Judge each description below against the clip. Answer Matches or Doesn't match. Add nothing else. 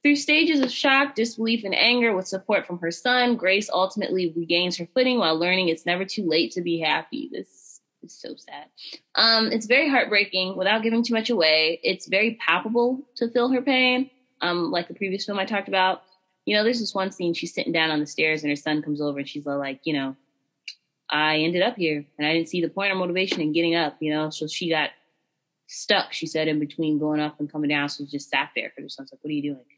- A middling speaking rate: Doesn't match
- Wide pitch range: Matches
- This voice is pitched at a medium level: Matches